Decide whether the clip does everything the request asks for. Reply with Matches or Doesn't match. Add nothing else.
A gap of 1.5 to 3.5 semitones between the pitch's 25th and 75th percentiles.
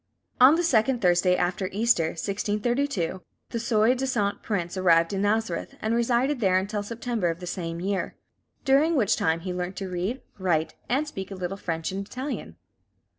Doesn't match